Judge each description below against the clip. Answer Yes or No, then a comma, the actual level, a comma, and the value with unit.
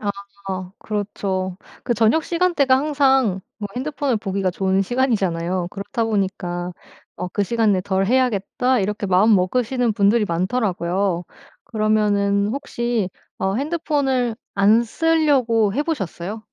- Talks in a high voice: Yes, high, 215 Hz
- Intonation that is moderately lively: Yes, average, 4.7 semitones